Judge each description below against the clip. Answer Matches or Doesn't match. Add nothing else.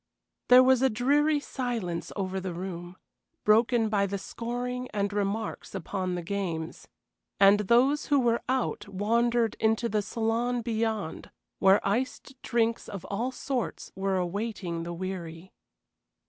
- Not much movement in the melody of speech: Doesn't match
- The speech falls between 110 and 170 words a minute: Matches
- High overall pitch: Matches